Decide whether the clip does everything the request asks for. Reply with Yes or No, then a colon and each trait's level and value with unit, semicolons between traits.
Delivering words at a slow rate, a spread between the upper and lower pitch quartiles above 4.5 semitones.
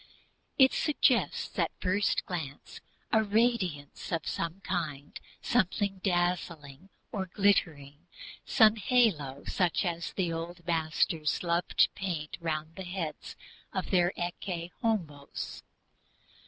No: slow, 110 wpm; average, 3.6 semitones